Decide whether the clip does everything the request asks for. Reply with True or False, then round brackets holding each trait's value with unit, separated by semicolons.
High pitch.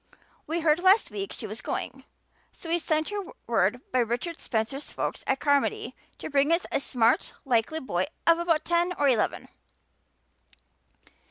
True (300 Hz)